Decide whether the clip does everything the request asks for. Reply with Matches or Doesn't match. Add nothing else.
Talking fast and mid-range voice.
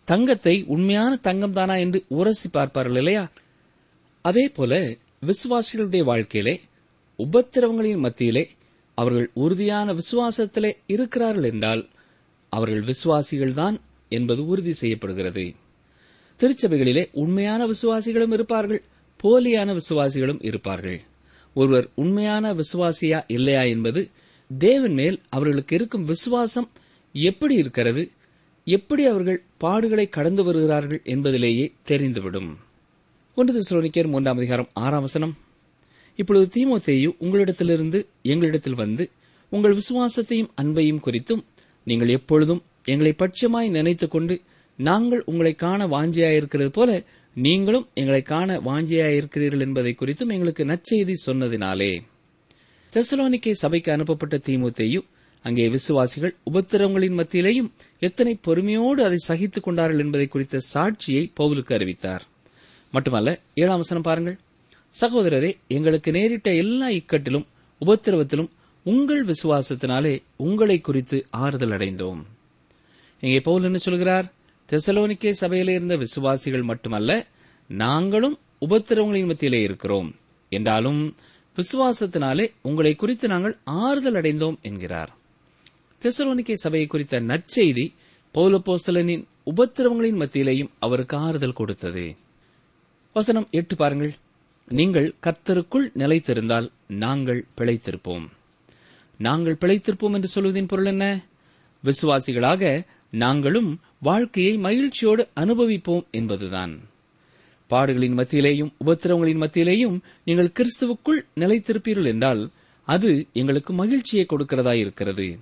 Doesn't match